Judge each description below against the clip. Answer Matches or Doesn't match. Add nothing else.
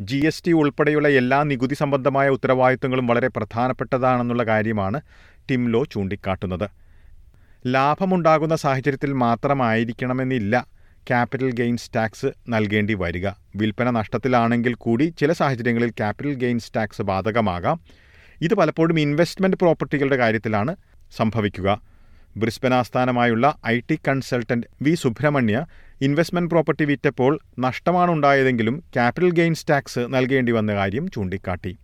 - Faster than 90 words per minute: Matches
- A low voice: Matches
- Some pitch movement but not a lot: Matches